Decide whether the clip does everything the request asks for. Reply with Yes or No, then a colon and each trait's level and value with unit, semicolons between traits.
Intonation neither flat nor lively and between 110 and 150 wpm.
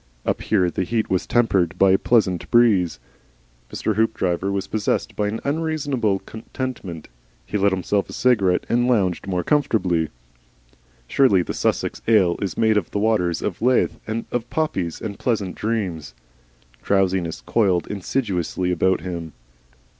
Yes: average, 4.1 semitones; average, 140 wpm